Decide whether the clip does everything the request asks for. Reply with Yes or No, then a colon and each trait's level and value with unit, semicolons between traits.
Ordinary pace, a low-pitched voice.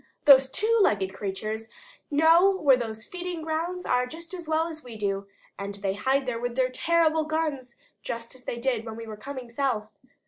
No: average, 195 wpm; very high, 260 Hz